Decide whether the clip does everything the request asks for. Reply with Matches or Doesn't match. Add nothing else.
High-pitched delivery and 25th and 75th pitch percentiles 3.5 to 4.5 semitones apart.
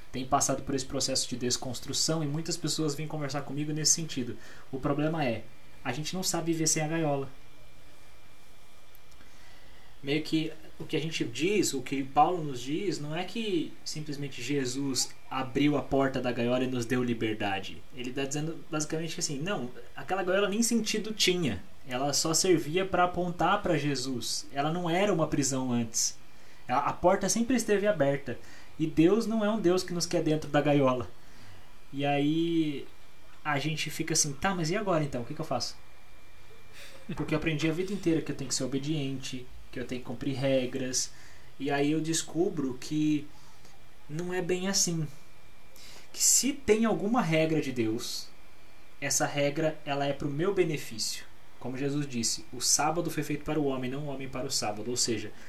Doesn't match